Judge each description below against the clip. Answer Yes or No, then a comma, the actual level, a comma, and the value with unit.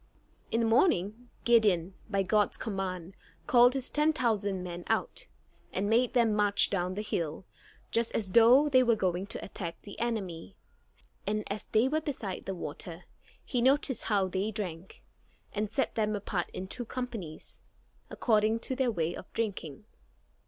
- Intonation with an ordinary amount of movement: Yes, average, 4.1 semitones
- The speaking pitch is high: Yes, high, 210 Hz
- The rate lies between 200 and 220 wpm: No, average, 160 wpm